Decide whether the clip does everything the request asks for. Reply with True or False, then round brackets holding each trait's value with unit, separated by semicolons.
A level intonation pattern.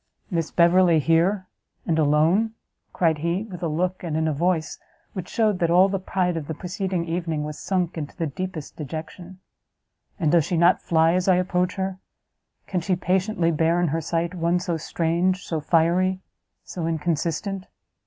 True (2.2 semitones)